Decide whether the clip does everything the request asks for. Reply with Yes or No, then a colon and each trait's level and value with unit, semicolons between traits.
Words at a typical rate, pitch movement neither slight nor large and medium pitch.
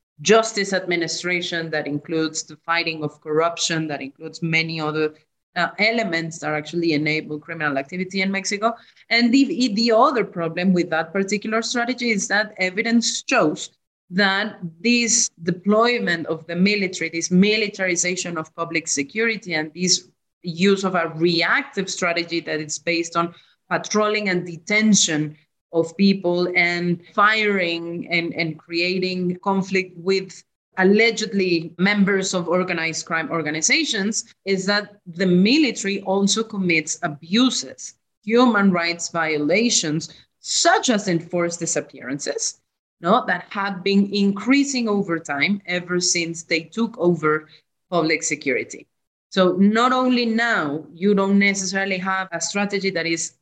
No: slow, 130 wpm; average, 3.8 semitones; medium, 180 Hz